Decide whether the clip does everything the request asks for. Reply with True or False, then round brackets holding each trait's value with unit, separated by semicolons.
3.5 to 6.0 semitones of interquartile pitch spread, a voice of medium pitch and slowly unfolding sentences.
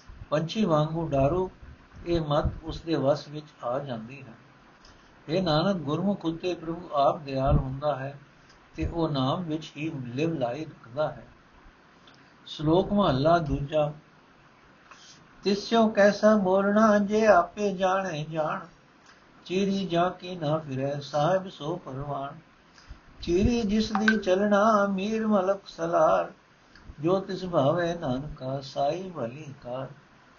False (5.1 semitones; 160 Hz; 115 wpm)